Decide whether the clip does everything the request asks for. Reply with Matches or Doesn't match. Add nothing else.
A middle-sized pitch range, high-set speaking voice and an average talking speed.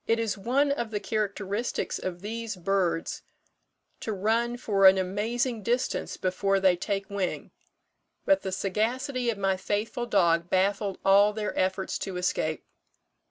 Matches